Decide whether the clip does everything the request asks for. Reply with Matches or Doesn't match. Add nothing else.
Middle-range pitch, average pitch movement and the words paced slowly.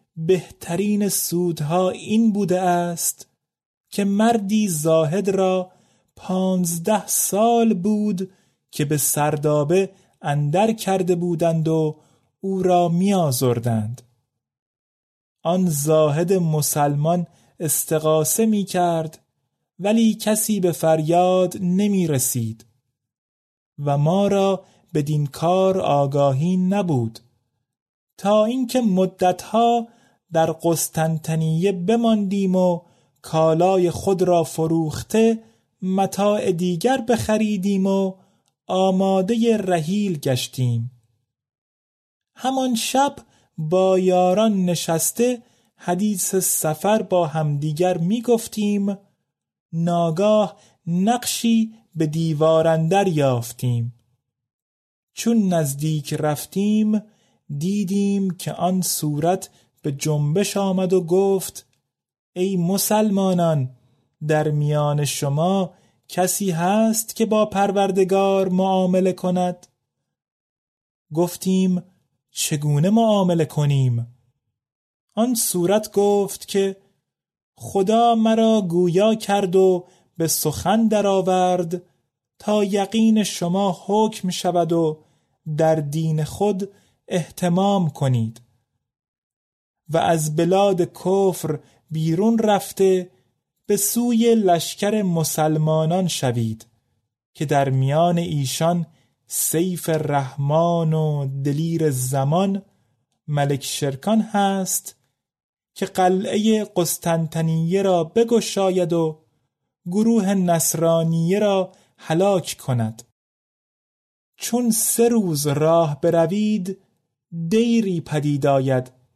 Matches